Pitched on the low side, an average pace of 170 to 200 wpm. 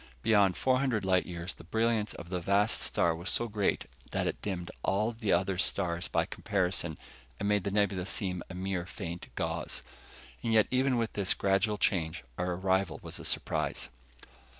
Yes: very low, 95 Hz; average, 180 wpm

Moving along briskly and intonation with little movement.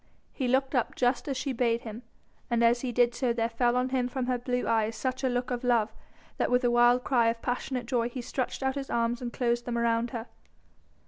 Yes: fast, 240 wpm; narrow, 1.4 semitones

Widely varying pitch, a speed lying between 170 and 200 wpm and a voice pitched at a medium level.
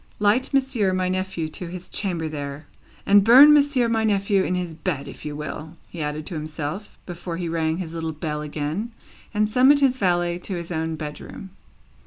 No: average, 4.8 semitones; average, 190 wpm; medium, 175 Hz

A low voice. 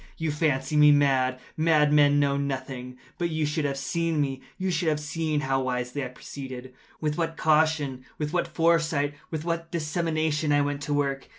No: medium, 150 Hz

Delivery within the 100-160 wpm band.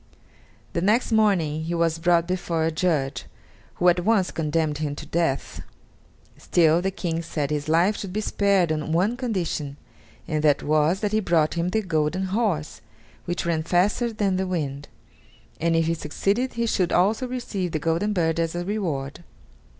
No: average, 175 wpm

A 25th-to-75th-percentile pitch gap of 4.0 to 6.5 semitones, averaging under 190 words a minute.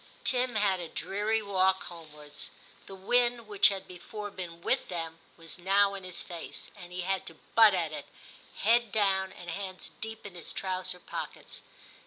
No: average, 2.8 semitones; average, 175 wpm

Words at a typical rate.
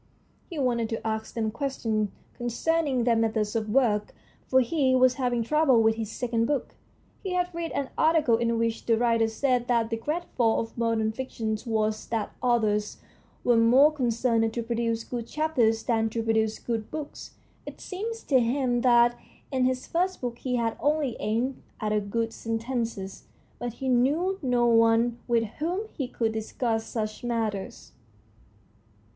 Yes: average, 165 wpm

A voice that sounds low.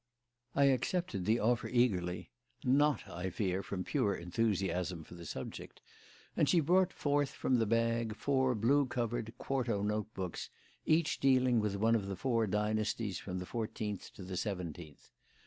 Yes: low, 110 Hz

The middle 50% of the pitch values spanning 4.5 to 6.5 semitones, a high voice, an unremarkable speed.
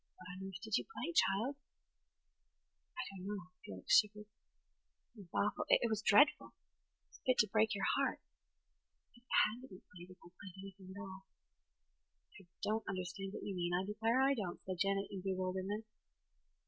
No: average, 2.7 semitones; high, 195 Hz; average, 175 wpm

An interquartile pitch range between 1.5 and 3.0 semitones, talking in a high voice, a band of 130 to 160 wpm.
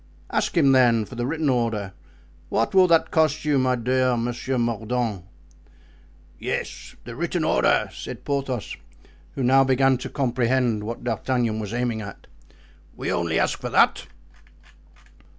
No: average, 2.7 semitones; low, 125 Hz; average, 145 wpm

